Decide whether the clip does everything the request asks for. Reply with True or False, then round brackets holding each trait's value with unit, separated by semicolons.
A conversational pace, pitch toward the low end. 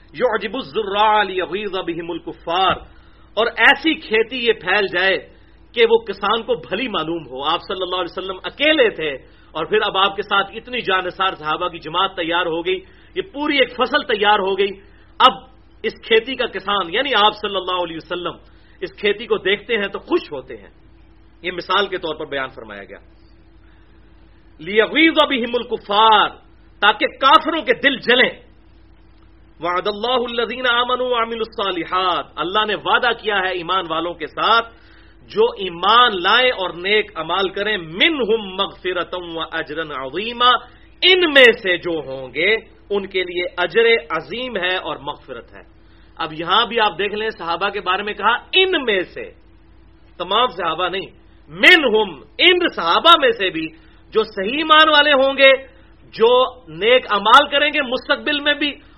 False (165 wpm; 205 Hz)